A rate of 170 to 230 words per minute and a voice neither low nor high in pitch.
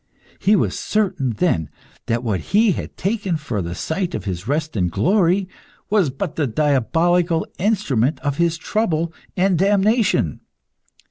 No: average, 145 wpm; medium, 165 Hz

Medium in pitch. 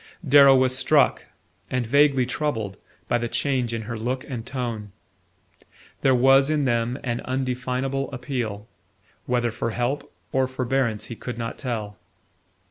No: low, 125 Hz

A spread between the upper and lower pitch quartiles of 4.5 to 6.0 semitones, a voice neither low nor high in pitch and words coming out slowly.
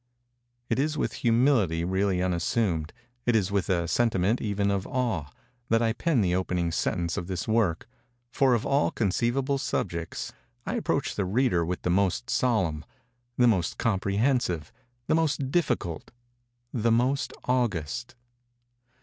No: average, 5.2 semitones; low, 115 Hz; slow, 125 wpm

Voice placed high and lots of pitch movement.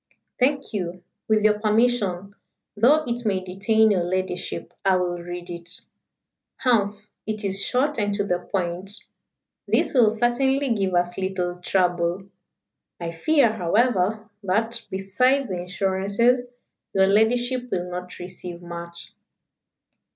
No: high, 195 Hz; average, 4.3 semitones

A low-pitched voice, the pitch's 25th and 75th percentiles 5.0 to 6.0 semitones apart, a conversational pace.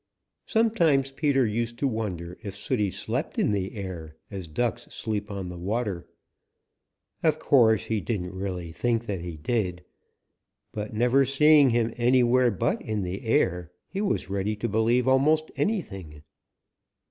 Yes: low, 110 Hz; wide, 5.4 semitones; average, 145 wpm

